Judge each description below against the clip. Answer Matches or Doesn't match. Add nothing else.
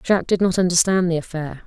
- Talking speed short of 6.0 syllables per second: Doesn't match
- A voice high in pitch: Doesn't match